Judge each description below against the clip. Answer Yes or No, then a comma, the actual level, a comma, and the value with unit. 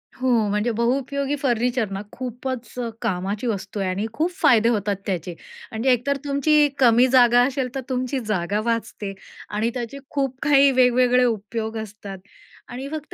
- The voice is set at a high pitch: Yes, high, 240 Hz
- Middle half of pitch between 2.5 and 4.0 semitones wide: Yes, average, 3.7 semitones